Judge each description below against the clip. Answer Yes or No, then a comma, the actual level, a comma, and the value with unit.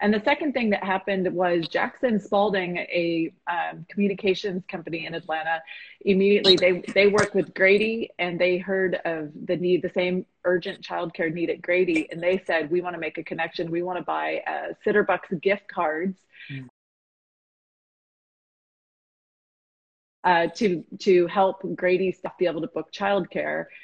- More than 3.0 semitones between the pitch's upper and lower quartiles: No, narrow, 2.6 semitones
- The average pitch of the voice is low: No, medium, 180 Hz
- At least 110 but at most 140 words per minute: No, average, 155 wpm